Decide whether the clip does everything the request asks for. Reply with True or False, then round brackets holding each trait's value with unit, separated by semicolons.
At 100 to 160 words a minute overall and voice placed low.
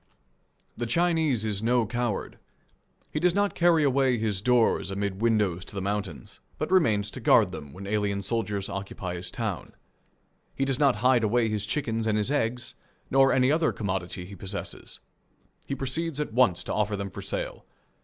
False (175 wpm; 110 Hz)